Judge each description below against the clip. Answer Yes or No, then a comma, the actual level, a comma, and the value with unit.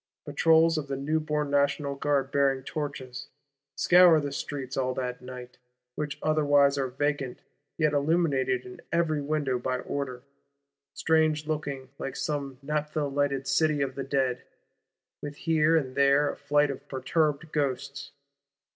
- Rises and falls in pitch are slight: Yes, narrow, 2.1 semitones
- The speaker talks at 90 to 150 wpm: Yes, average, 140 wpm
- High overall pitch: No, medium, 140 Hz